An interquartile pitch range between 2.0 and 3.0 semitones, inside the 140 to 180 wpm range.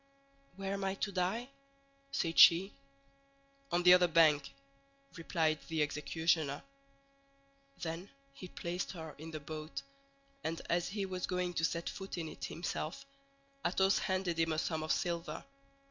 Yes: narrow, 2.4 semitones; average, 145 wpm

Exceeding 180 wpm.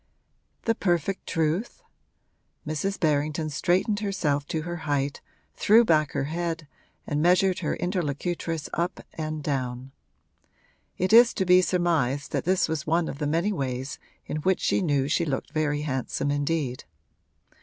No: average, 145 wpm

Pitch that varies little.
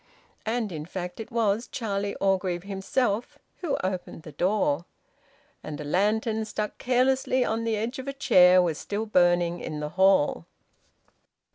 No: average, 4.3 semitones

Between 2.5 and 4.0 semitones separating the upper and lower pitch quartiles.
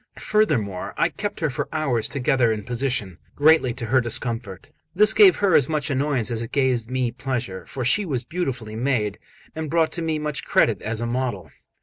No: average, 4.8 semitones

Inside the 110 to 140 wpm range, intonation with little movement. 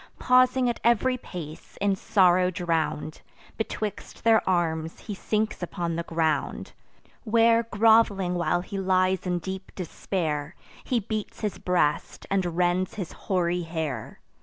No: slow, 135 wpm; average, 4.0 semitones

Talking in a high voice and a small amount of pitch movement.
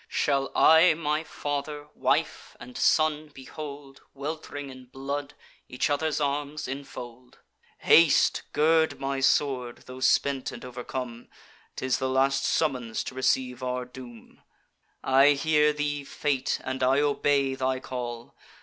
No: low, 135 Hz; narrow, 2.3 semitones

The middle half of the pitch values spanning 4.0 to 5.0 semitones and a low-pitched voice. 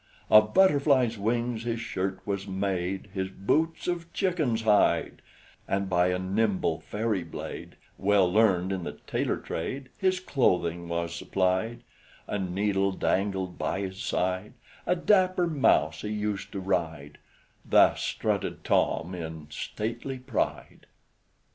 Yes: average, 4.3 semitones; low, 100 Hz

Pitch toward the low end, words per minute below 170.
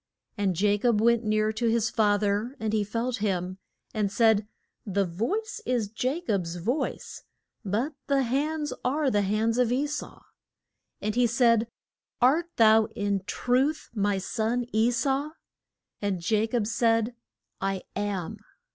No: high, 225 Hz; average, 150 wpm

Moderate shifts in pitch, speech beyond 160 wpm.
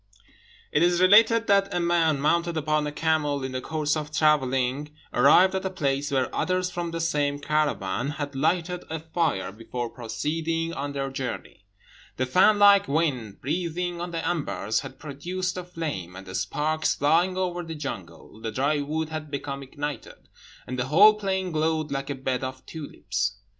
Yes: average, 4.2 semitones; average, 175 wpm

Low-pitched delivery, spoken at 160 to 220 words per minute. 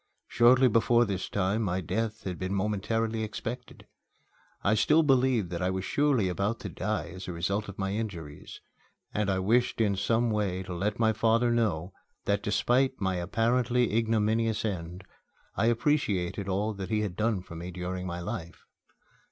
Yes: low, 105 Hz; average, 170 wpm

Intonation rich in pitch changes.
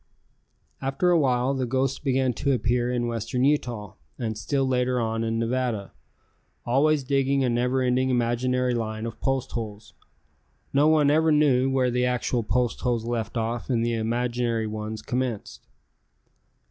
No: narrow, 2.4 semitones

